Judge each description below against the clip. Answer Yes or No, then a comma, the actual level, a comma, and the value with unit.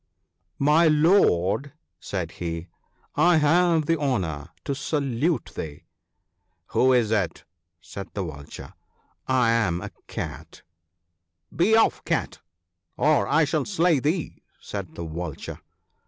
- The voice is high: No, low, 125 Hz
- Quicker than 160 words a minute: No, average, 140 wpm